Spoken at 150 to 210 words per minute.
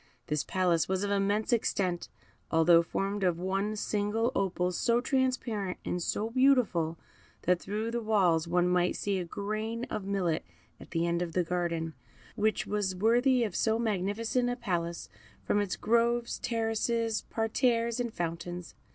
Yes: average, 155 wpm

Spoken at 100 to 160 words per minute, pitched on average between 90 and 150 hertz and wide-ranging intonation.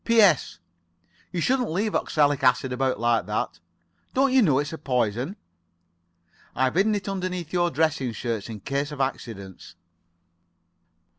Yes: slow, 135 wpm; medium, 140 Hz; wide, 7.4 semitones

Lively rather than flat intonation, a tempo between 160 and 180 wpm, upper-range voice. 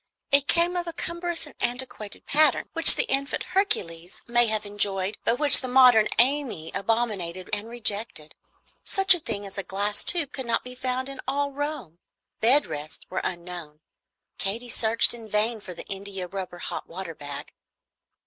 Yes: wide, 6.1 semitones; average, 170 wpm; high, 225 Hz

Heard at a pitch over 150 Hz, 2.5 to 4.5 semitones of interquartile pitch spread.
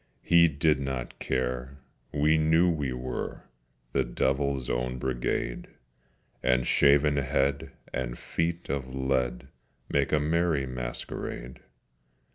No: very low, 65 Hz; average, 2.9 semitones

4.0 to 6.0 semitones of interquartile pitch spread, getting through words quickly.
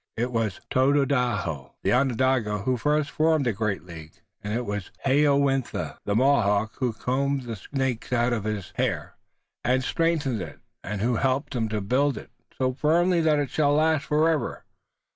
No: average, 4.7 semitones; average, 170 wpm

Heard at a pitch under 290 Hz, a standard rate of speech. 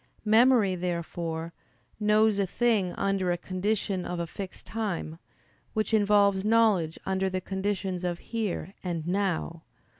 No: high, 190 Hz; slow, 130 wpm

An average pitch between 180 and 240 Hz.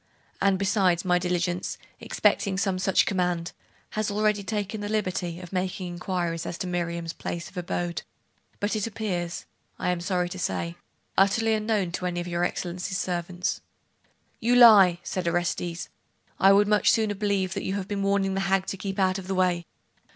Yes: medium, 185 Hz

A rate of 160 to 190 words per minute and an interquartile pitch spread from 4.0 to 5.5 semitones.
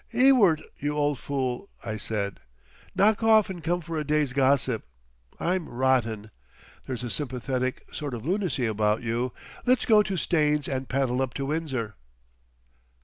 No: average, 150 wpm; average, 5.1 semitones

